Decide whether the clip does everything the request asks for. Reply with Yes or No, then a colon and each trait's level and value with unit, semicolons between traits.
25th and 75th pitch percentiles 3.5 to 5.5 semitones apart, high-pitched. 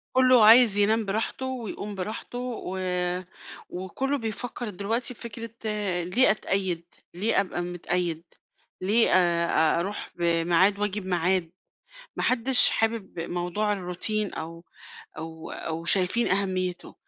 Yes: average, 4.1 semitones; high, 195 Hz